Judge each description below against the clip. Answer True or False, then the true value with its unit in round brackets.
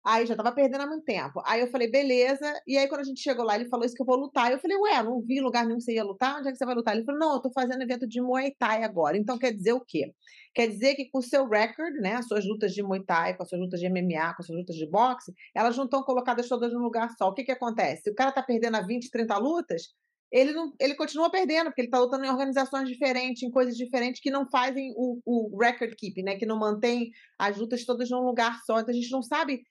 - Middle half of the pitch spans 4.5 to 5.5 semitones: False (2.9 semitones)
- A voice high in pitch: True (250 Hz)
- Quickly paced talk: True (290 wpm)